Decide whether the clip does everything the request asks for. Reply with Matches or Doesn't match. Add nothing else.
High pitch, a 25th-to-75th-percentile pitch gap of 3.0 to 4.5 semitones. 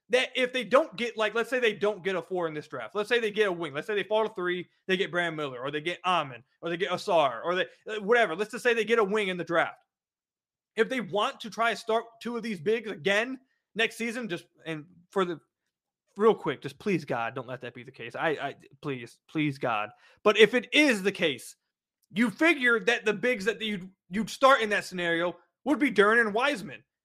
Doesn't match